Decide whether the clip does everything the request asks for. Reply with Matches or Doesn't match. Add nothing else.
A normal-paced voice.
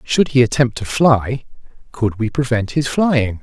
Matches